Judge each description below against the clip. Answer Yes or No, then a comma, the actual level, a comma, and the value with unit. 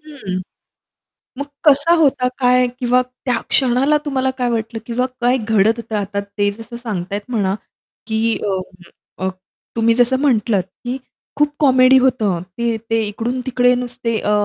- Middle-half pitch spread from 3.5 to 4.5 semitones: No, average, 2.8 semitones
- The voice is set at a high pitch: Yes, high, 240 Hz